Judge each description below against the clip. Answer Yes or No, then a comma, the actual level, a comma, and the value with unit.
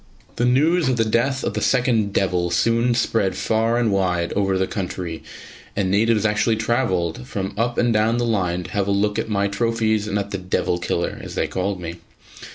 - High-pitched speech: No, low, 105 Hz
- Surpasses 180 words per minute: Yes, fast, 205 wpm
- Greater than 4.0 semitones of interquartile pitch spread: No, average, 3.6 semitones